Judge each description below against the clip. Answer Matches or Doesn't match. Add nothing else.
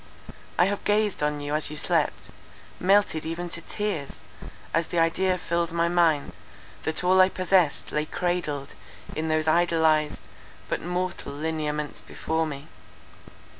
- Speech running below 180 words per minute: Matches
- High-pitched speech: Doesn't match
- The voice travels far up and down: Doesn't match